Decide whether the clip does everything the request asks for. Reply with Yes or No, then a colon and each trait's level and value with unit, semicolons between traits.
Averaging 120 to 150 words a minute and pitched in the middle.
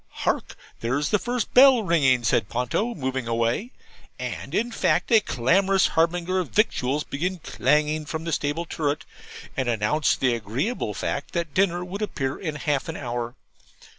No: average, 160 wpm; medium, 150 Hz